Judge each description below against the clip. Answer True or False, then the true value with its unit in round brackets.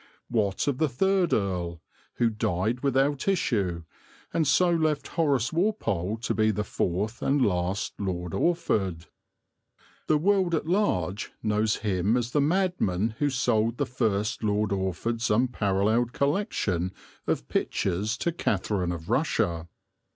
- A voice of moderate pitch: False (110 Hz)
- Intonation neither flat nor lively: False (7.0 semitones)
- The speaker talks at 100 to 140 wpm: True (135 wpm)